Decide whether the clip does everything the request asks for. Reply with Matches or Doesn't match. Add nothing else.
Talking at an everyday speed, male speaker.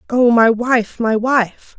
Doesn't match